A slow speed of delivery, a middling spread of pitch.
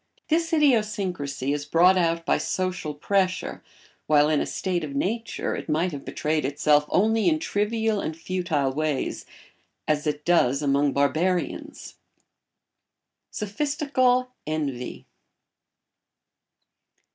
No: slow, 115 wpm; wide, 5.8 semitones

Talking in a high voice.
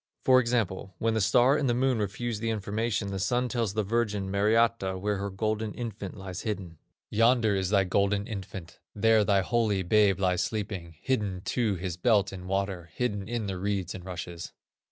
No: low, 100 Hz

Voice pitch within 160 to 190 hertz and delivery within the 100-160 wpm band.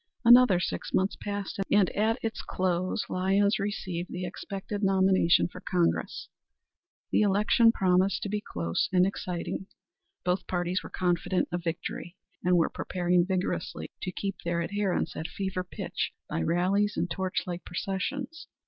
Yes: medium, 185 Hz; average, 150 wpm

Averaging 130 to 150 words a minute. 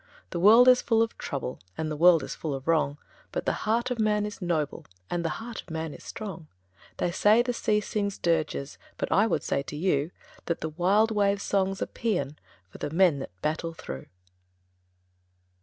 No: average, 200 wpm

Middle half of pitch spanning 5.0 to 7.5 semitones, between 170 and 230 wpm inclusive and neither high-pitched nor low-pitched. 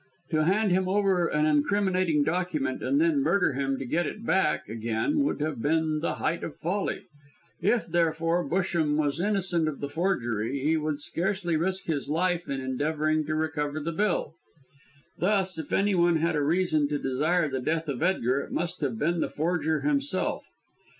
No: average, 3.8 semitones; average, 175 wpm; medium, 160 Hz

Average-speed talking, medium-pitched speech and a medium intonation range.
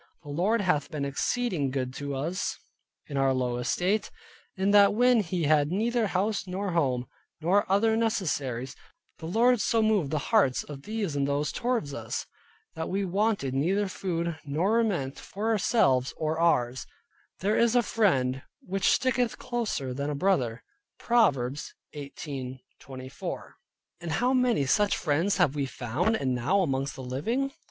No: average, 155 wpm; medium, 170 Hz; wide, 7.4 semitones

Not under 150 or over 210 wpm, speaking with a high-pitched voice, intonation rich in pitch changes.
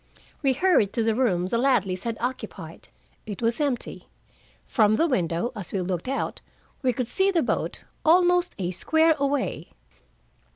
Yes: average, 160 wpm; high, 245 Hz; wide, 6.3 semitones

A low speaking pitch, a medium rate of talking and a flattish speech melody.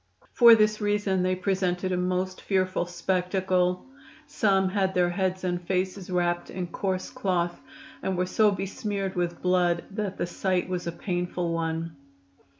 No: medium, 185 Hz; average, 150 wpm; narrow, 1.5 semitones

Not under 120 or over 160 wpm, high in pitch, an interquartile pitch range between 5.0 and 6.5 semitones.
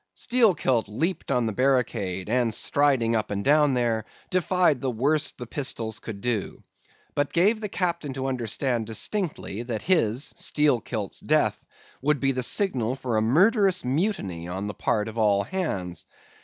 No: average, 155 wpm; low, 125 Hz; wide, 5.6 semitones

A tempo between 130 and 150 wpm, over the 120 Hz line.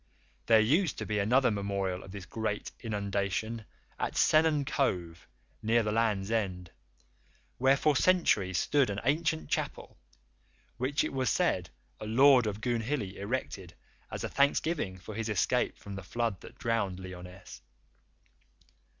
No: average, 140 wpm; low, 110 Hz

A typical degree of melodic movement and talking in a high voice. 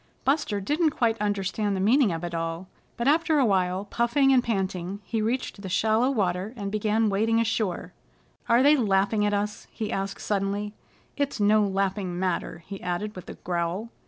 Yes: average, 3.2 semitones; high, 205 Hz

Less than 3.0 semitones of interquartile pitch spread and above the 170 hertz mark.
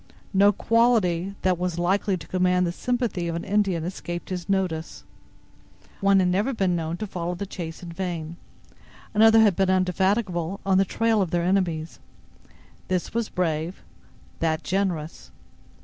Yes: narrow, 2.5 semitones; medium, 185 Hz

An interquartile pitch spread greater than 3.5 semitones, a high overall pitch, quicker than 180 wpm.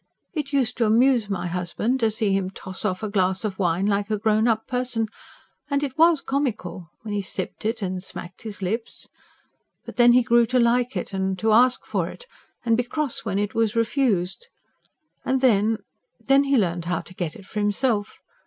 Yes: average, 4.2 semitones; high, 220 Hz; average, 200 wpm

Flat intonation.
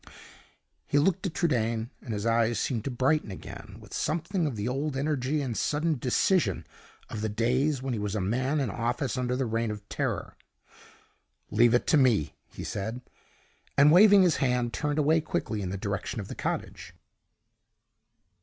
No: average, 5.0 semitones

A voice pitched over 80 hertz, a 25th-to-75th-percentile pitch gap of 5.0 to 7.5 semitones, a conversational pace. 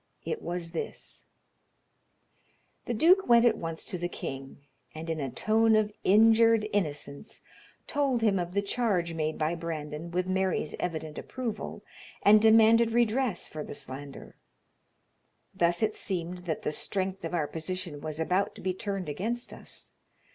Yes: medium, 185 Hz; average, 5.3 semitones; average, 155 wpm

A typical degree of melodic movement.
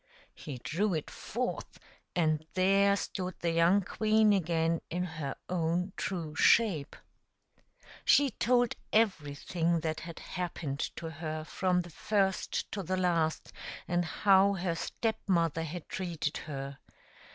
Yes: average, 3.5 semitones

